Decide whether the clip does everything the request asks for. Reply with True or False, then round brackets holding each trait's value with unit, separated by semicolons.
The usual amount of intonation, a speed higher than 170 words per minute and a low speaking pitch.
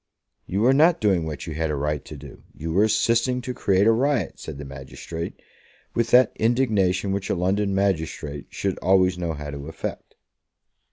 False (5.9 semitones; 185 wpm; 95 Hz)